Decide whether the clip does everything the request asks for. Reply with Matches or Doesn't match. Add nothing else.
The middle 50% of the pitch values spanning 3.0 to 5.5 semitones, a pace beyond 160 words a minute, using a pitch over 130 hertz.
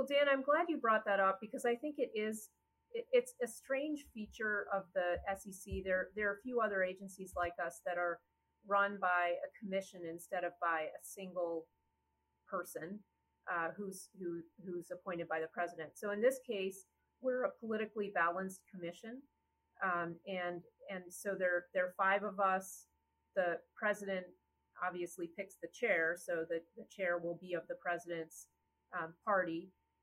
Matches